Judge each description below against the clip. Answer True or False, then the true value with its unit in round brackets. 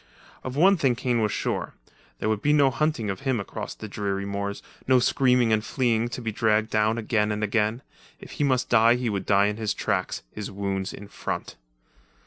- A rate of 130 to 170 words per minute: False (205 wpm)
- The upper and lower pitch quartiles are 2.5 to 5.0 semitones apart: True (3.4 semitones)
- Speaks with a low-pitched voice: True (110 Hz)